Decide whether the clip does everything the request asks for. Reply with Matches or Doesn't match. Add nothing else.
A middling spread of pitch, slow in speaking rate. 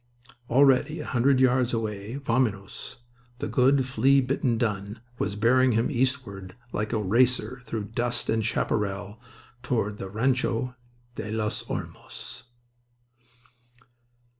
Matches